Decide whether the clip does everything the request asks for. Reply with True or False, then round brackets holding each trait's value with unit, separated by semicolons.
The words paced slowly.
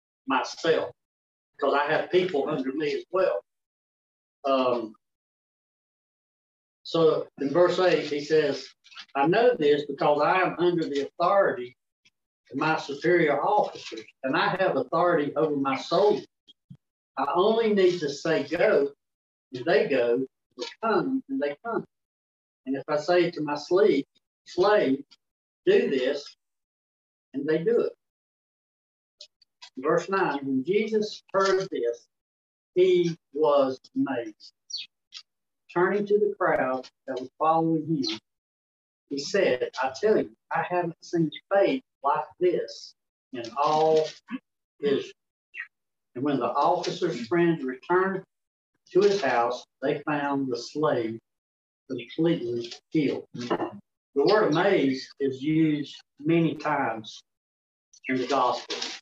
True (120 wpm)